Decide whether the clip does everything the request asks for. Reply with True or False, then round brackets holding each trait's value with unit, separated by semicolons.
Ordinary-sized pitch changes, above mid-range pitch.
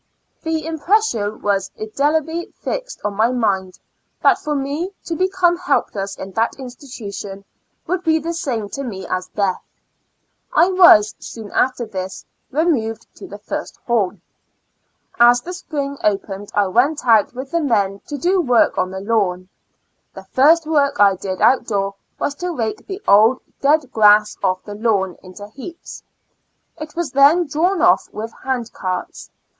False (7.6 semitones; 240 Hz)